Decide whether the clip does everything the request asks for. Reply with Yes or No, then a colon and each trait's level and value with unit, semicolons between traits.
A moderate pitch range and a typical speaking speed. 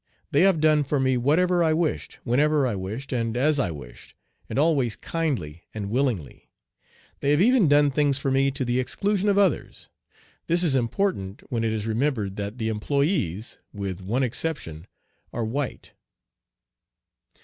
No: wide, 5.8 semitones; average, 160 wpm